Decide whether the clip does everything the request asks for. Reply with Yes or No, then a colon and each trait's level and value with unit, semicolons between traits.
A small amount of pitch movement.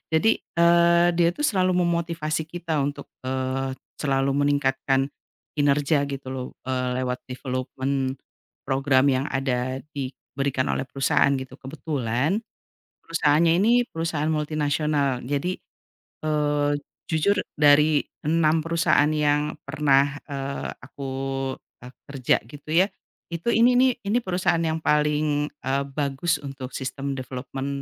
No: average, 3.2 semitones